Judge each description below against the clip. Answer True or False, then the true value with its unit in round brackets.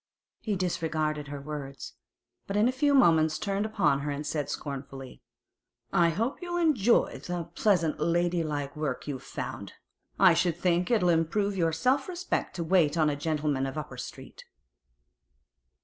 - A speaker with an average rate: True (155 wpm)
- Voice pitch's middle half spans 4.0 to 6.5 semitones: True (4.9 semitones)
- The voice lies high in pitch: False (165 Hz)